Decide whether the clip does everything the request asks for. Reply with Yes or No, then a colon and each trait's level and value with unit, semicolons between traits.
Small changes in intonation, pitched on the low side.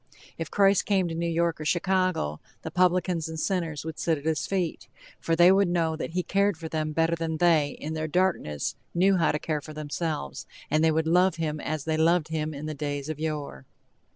No: narrow, 2.3 semitones; medium, 160 Hz